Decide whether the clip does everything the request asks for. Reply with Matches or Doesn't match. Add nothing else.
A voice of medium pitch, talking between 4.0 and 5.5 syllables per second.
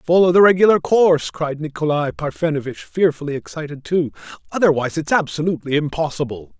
Doesn't match